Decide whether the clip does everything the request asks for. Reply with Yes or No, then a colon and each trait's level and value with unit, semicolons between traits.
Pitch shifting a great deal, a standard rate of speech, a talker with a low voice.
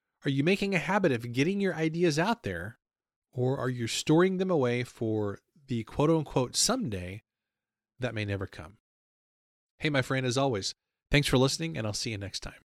Yes: wide, 6.3 semitones; average, 190 wpm; low, 130 Hz